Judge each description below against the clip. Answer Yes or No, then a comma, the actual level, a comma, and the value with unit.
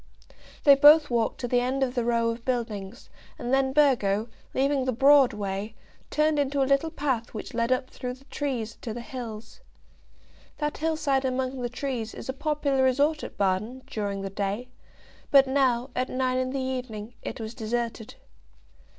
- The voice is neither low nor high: No, very high, 255 Hz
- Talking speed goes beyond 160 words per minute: Yes, average, 175 wpm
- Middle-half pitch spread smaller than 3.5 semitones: Yes, average, 3.1 semitones